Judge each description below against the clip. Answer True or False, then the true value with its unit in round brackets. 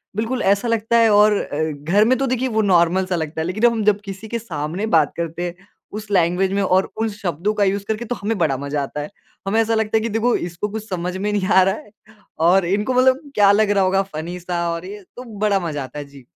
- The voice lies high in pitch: True (195 Hz)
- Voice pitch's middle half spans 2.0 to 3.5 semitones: False (4.1 semitones)